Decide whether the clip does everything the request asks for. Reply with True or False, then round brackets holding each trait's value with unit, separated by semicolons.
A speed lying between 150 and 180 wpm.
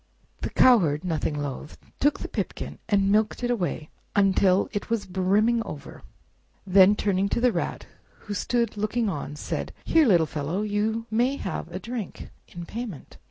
True (160 wpm)